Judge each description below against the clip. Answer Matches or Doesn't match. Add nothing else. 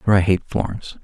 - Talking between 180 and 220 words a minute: Doesn't match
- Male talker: Matches